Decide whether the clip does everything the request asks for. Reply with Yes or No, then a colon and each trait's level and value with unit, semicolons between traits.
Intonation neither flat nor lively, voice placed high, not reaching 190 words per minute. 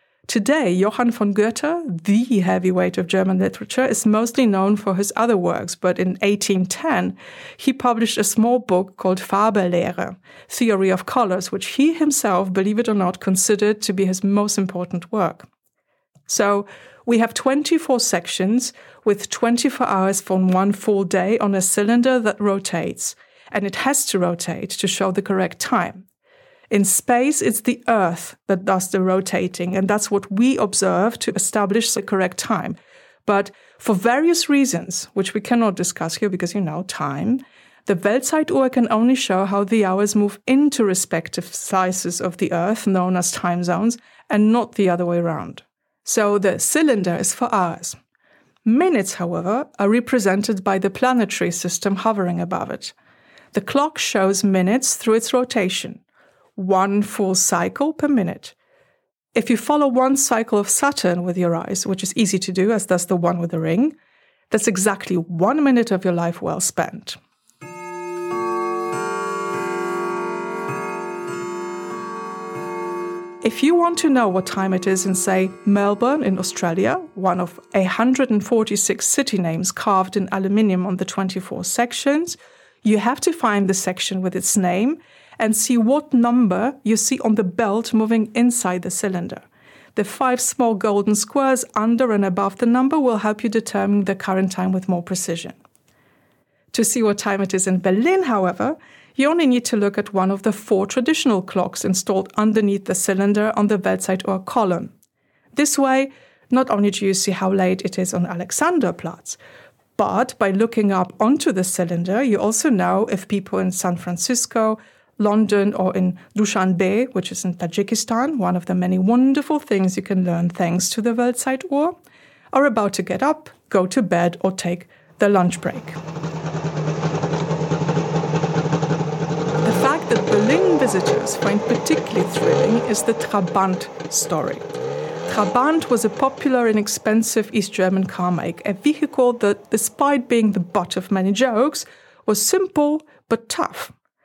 Yes: average, 4.4 semitones; high, 205 Hz; average, 160 wpm